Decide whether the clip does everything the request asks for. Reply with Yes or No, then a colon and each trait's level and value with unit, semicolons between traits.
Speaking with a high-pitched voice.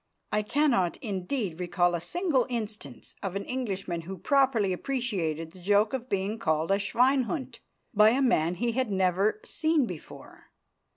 Yes: high, 205 Hz